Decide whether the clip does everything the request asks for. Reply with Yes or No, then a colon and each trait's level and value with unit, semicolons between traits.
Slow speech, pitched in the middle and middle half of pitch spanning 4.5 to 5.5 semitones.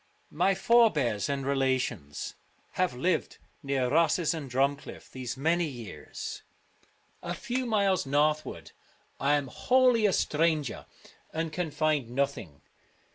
Yes: slow, 120 wpm; medium, 150 Hz; average, 4.8 semitones